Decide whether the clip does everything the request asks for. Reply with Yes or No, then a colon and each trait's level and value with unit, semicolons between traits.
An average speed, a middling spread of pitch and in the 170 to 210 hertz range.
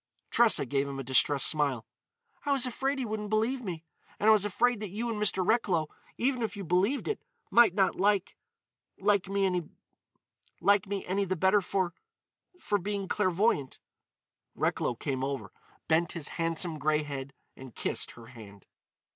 No: average, 155 wpm; wide, 5.8 semitones; high, 190 Hz